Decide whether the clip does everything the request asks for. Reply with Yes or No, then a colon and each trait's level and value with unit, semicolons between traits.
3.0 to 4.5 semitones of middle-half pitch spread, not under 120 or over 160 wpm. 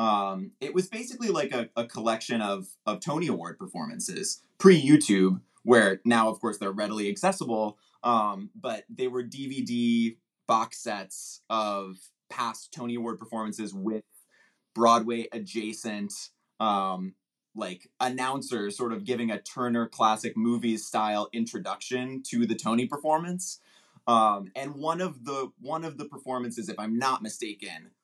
Yes: average, 3.5 semitones; average, 140 wpm